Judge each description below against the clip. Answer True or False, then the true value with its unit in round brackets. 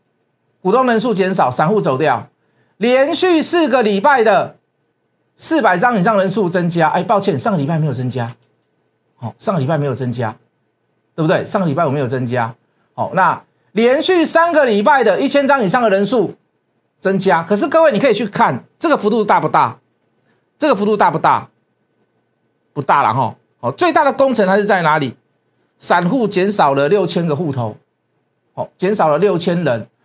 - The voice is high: True (195 Hz)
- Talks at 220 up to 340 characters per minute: True (270 characters per minute)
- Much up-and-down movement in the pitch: True (8.4 semitones)